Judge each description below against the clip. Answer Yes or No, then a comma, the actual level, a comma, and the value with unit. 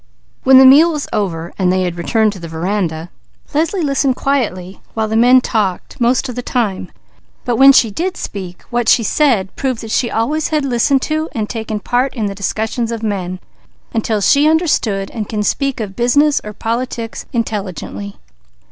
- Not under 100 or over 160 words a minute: No, average, 185 wpm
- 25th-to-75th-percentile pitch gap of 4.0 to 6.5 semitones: Yes, average, 5.0 semitones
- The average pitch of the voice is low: No, high, 225 Hz